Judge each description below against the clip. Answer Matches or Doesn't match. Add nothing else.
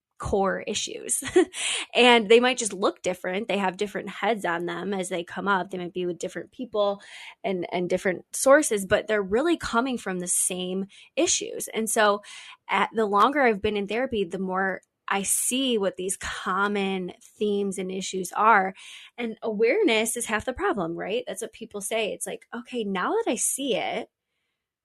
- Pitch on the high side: Matches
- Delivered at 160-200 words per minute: Matches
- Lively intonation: Doesn't match